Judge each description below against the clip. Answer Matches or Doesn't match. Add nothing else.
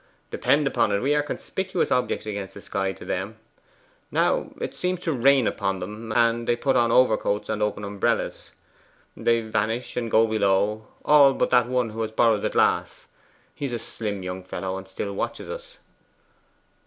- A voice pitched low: Matches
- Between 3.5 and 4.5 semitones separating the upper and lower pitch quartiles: Matches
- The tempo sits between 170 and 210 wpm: Matches